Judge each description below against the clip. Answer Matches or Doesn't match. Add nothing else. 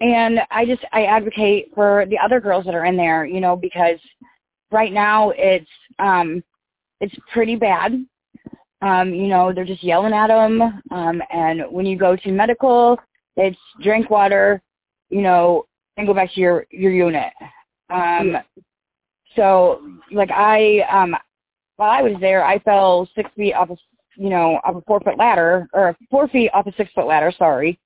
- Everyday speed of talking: Matches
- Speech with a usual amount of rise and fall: Matches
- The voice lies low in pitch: Doesn't match